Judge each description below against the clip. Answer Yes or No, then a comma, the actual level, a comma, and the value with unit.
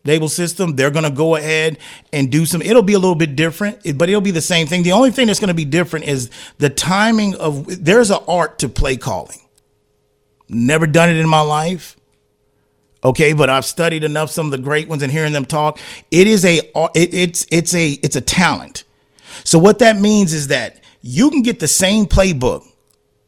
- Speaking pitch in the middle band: Yes, medium, 160 Hz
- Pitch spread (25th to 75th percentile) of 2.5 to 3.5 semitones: No, average, 4.0 semitones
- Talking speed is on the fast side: Yes, fast, 210 wpm